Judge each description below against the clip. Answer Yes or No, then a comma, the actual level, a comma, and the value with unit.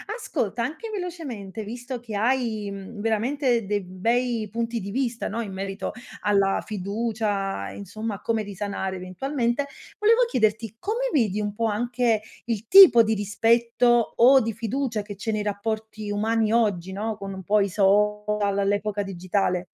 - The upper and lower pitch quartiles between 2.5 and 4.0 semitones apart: Yes, average, 2.8 semitones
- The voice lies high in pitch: Yes, high, 215 Hz